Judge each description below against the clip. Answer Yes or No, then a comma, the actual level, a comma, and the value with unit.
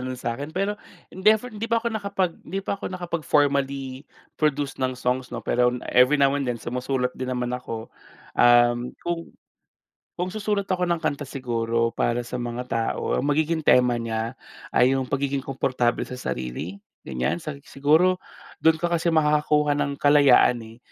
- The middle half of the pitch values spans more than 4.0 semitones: Yes, average, 4.8 semitones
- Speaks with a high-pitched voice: No, medium, 140 Hz